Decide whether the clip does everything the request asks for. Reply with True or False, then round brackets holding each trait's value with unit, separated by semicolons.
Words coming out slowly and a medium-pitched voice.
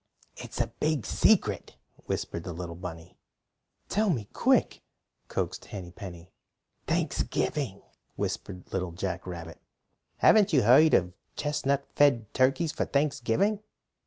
False (120 wpm; 110 Hz)